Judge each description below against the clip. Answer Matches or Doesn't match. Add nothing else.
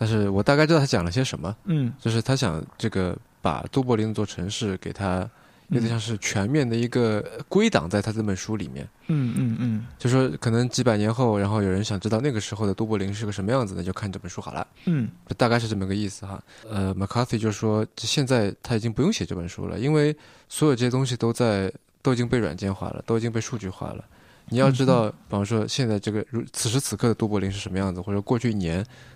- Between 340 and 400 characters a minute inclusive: Matches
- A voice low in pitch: Matches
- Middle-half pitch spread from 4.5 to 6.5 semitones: Doesn't match